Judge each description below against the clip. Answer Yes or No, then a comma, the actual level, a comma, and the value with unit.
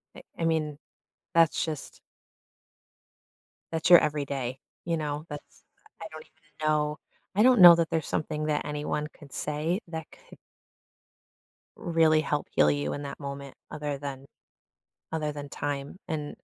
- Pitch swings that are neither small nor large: No, narrow, 2.0 semitones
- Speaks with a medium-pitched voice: Yes, medium, 150 Hz